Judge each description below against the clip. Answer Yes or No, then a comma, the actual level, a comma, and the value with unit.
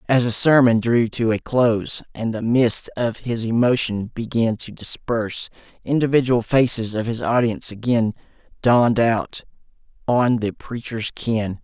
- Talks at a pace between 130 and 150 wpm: Yes, average, 145 wpm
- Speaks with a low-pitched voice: Yes, low, 115 Hz